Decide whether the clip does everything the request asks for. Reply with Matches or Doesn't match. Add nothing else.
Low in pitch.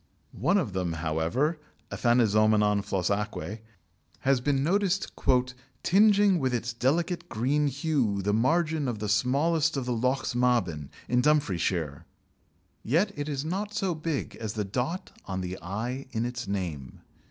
Matches